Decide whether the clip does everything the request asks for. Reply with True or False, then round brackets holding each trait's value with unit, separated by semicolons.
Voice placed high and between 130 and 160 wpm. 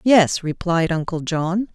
False (175 Hz; 140 wpm)